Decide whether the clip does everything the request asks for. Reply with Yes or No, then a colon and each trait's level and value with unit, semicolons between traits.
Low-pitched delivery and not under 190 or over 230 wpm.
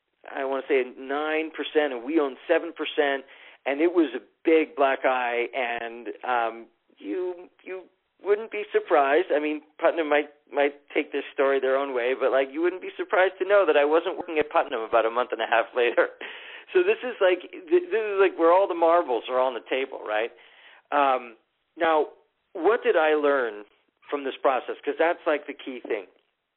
No: medium, 155 Hz; average, 200 wpm